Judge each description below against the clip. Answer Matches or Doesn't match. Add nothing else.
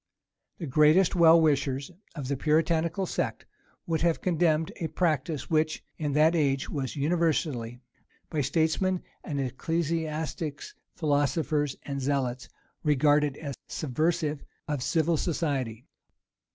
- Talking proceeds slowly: Matches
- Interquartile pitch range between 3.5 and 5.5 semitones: Doesn't match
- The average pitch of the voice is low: Doesn't match